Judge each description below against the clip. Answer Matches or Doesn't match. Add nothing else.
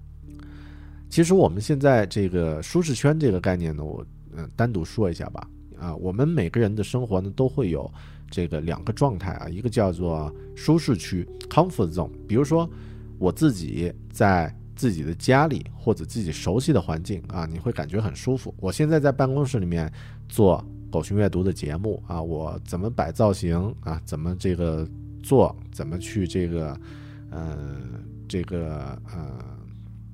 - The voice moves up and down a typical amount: Doesn't match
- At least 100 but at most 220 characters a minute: Doesn't match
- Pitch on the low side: Matches